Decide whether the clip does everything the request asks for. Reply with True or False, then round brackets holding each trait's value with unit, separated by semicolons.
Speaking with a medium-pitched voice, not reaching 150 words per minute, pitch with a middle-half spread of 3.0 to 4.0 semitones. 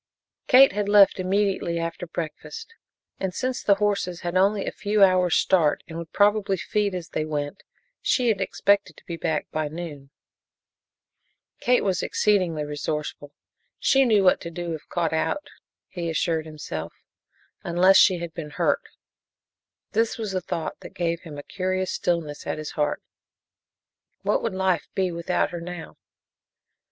False (180 Hz; 160 wpm; 3.6 semitones)